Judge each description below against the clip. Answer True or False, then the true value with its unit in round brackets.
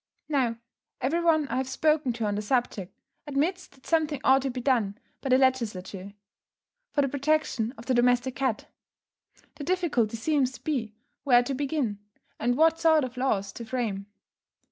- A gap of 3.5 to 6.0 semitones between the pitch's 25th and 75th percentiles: True (4.1 semitones)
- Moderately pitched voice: False (260 Hz)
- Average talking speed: True (170 wpm)